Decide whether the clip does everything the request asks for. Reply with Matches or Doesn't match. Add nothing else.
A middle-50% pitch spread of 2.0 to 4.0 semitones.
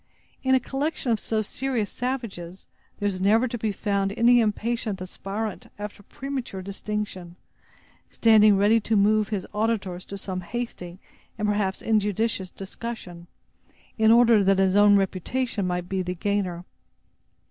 Matches